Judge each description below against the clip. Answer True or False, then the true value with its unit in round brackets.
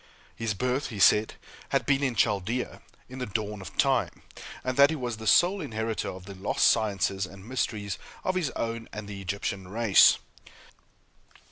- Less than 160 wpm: False (170 wpm)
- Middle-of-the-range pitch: False (110 Hz)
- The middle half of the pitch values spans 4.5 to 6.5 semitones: False (4.1 semitones)